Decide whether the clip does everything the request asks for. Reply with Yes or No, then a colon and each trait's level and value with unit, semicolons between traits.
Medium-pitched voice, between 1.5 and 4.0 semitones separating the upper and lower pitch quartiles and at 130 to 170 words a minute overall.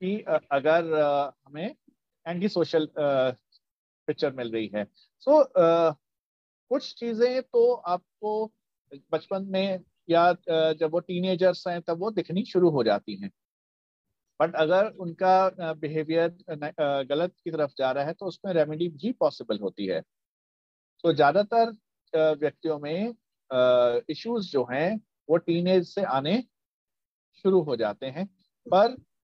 No: medium, 165 Hz; average, 4.8 semitones; average, 135 wpm